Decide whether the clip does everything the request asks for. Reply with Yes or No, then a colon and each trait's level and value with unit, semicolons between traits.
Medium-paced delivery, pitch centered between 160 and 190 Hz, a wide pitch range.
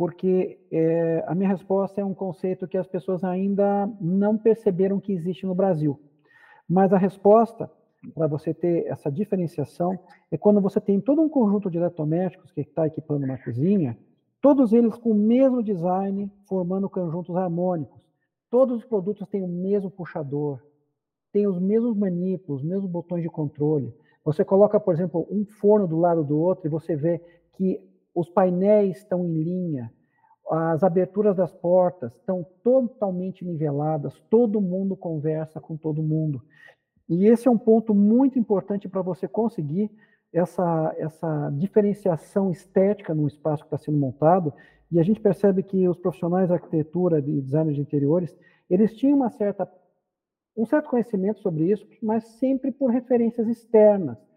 No: average, 160 wpm; medium, 185 Hz; average, 4.2 semitones